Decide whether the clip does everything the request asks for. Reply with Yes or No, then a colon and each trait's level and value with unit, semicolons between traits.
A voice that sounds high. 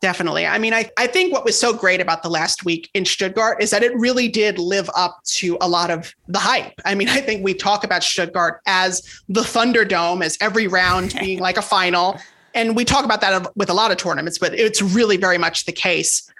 Yes: high, 195 Hz